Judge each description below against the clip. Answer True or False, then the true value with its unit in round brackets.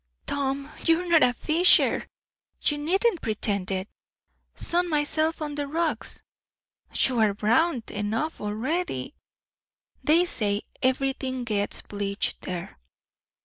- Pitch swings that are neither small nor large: False (7.3 semitones)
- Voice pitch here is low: False (270 Hz)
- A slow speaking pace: True (110 wpm)